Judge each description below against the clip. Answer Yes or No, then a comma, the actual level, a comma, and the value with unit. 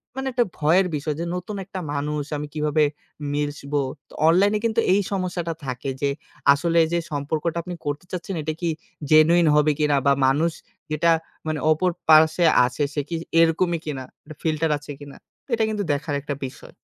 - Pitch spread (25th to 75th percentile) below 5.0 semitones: Yes, average, 2.9 semitones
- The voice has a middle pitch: Yes, medium, 155 Hz